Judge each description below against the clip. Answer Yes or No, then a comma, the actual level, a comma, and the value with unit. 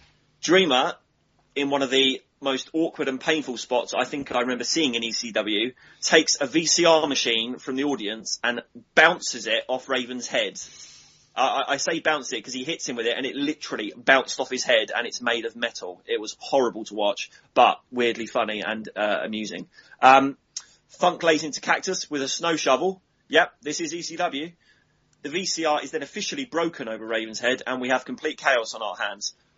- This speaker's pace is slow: No, average, 190 wpm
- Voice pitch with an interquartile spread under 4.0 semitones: No, average, 4.6 semitones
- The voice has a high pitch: No, low, 135 Hz